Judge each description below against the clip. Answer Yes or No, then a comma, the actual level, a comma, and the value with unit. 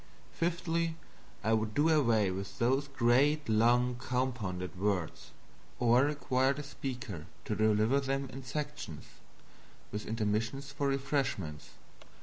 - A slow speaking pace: Yes, slow, 120 wpm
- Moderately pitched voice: No, low, 125 Hz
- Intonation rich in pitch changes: No, average, 4.5 semitones